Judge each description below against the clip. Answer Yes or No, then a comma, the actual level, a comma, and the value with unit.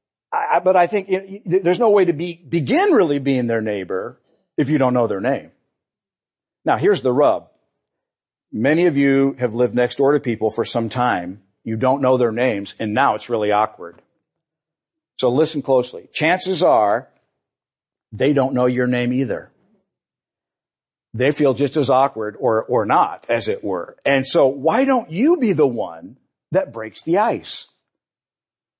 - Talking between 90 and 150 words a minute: No, average, 170 wpm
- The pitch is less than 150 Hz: Yes, low, 135 Hz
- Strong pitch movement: Yes, wide, 5.7 semitones